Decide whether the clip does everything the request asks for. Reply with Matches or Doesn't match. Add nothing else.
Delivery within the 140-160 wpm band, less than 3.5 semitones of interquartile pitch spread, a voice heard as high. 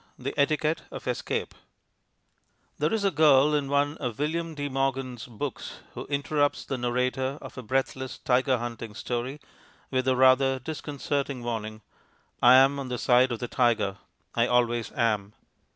Doesn't match